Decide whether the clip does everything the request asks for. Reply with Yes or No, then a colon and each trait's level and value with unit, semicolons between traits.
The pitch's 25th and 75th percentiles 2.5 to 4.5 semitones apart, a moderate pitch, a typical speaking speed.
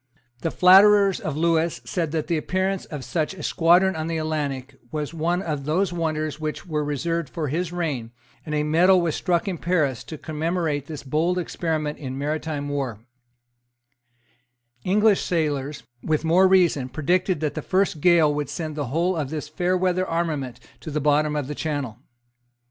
Yes: average, 3.0 semitones; medium, 155 Hz; average, 170 wpm